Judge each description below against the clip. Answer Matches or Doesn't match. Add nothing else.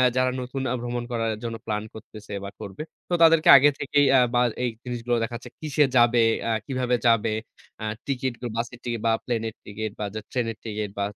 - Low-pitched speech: Matches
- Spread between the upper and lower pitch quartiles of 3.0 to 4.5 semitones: Doesn't match